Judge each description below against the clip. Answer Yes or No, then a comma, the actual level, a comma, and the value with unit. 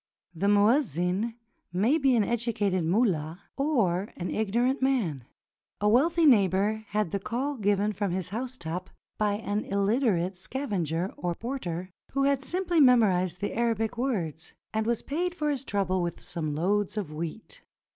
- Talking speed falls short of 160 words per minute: Yes, average, 150 wpm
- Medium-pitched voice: No, high, 210 Hz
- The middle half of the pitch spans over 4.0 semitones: Yes, wide, 5.5 semitones